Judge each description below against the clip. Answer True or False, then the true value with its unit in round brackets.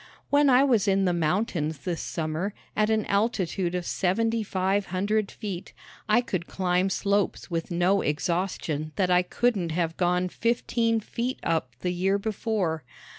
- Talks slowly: False (155 wpm)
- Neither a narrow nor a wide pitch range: True (3.7 semitones)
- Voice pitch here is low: False (190 Hz)